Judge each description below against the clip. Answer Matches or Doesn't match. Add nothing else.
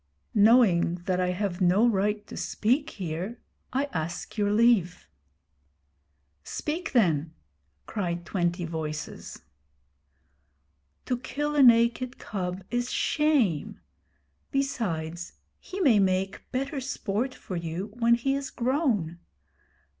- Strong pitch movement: Matches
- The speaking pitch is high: Matches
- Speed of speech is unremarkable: Doesn't match